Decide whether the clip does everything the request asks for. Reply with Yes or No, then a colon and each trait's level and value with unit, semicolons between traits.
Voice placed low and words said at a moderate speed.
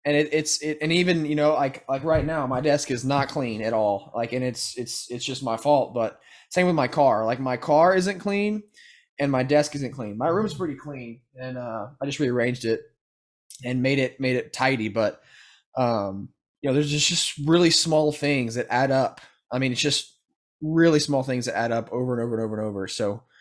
No: low, 130 Hz; fast, 230 wpm